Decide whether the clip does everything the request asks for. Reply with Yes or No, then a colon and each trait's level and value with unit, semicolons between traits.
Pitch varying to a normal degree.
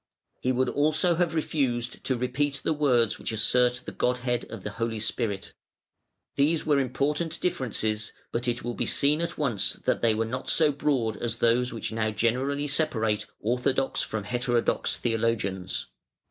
Yes: average, 3.9 semitones